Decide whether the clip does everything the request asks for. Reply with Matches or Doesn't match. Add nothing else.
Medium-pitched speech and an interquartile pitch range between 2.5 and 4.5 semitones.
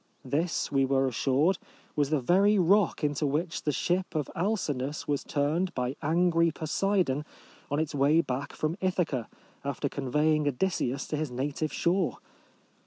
Matches